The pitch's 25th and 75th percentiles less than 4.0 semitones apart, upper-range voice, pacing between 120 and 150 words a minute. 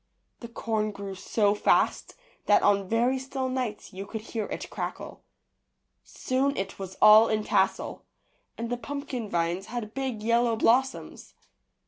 Yes: average, 3.5 semitones; high, 225 Hz; average, 145 wpm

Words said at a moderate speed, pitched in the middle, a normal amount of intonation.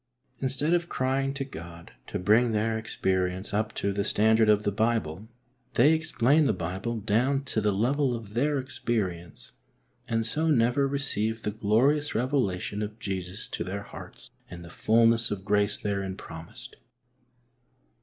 No: average, 155 wpm; low, 110 Hz; average, 4.6 semitones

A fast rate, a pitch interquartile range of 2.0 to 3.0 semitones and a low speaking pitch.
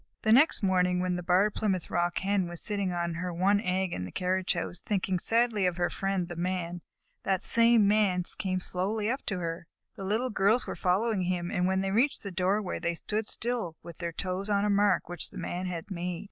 No: fast, 220 wpm; narrow, 2.5 semitones; medium, 185 Hz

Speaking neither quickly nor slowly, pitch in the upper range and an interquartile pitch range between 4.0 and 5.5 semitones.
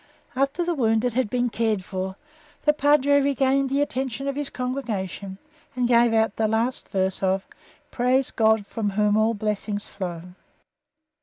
Yes: average, 155 wpm; high, 230 Hz; average, 4.5 semitones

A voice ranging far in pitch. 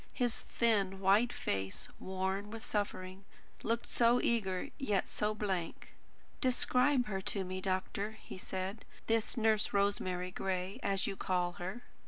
No: average, 3.0 semitones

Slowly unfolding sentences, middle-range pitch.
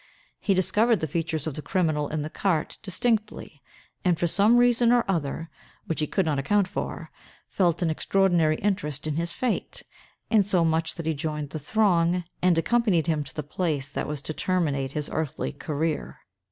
No: average, 175 wpm; medium, 165 Hz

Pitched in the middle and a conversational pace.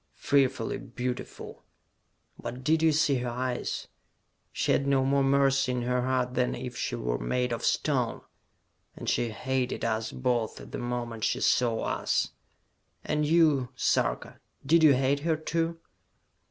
No: low, 130 Hz; average, 150 wpm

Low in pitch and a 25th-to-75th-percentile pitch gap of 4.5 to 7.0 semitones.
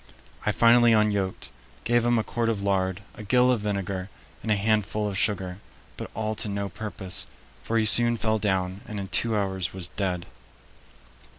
No: low, 105 Hz; average, 2.7 semitones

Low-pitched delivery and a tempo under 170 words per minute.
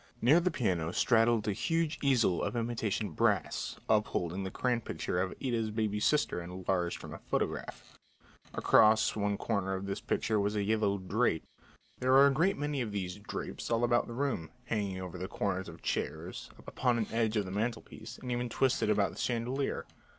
No: low, 110 Hz; average, 190 wpm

